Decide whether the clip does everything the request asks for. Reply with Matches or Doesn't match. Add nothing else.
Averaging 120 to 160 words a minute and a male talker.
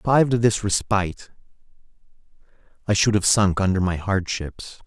Matches